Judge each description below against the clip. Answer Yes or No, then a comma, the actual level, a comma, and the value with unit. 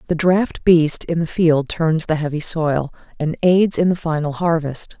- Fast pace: No, average, 190 wpm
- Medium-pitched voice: Yes, medium, 160 Hz